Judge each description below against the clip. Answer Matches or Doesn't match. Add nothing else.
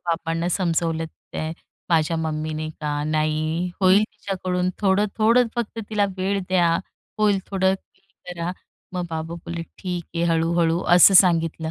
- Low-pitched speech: Doesn't match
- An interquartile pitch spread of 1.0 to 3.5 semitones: Matches